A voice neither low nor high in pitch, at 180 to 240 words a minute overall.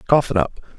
No: low, 115 Hz; fast, 230 wpm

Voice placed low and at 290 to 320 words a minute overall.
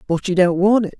No: high, 190 Hz; fast, 300 wpm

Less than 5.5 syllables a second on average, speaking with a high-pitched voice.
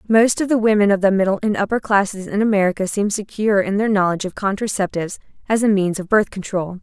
No: 6.5 syllables/s; high, 200 Hz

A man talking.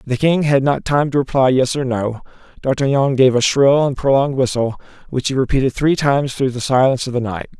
Yes: male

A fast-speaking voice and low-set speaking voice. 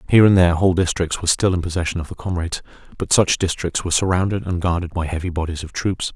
Yes: fast, 235 wpm; very low, 90 Hz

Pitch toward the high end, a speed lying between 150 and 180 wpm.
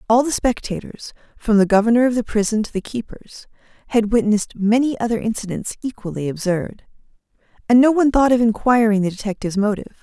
Yes: high, 220 Hz; average, 170 wpm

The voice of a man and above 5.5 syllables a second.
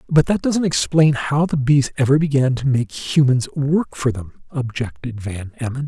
No: male; 4.6 syllables/s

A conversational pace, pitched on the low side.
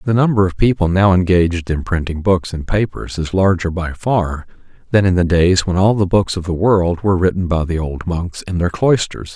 No: fast, 225 wpm; very low, 90 Hz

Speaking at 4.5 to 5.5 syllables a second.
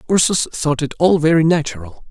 No: 5.7 syllables/s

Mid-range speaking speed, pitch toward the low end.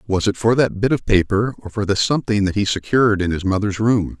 No: fast, 255 wpm; low, 105 Hz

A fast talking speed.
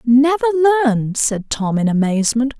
No: average, 140 wpm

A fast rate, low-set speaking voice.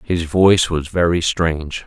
No: average, 160 wpm; very low, 85 Hz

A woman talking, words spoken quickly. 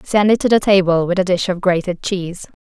Yes: female; fast, 250 wpm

